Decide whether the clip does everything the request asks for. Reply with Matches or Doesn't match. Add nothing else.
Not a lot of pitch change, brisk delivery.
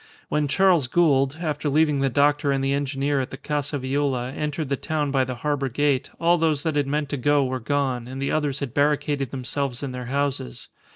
Matches